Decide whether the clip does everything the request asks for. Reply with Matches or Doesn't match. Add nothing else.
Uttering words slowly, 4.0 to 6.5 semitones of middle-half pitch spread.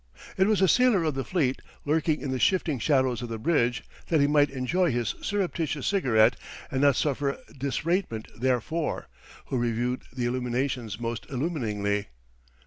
Doesn't match